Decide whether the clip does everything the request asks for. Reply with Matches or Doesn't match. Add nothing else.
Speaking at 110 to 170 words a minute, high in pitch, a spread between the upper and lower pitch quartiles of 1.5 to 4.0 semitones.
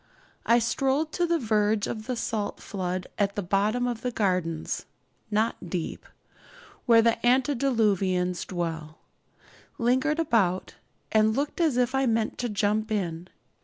Doesn't match